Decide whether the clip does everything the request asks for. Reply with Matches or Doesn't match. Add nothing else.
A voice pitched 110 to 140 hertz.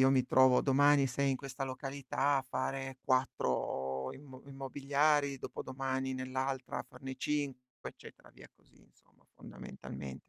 Matches